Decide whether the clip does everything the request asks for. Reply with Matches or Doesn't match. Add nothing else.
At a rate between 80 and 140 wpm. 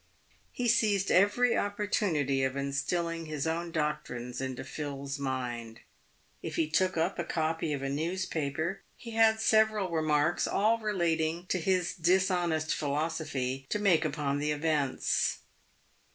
Matches